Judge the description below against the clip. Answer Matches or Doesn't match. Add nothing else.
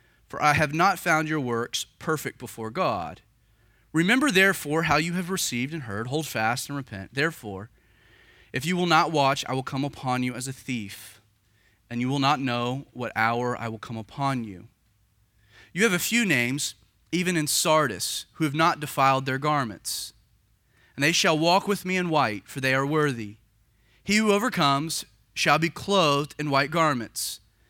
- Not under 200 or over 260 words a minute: Doesn't match